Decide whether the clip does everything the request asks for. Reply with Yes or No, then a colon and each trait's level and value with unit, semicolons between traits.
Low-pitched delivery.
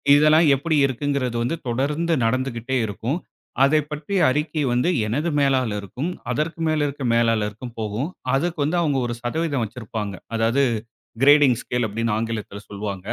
Yes: low, 130 Hz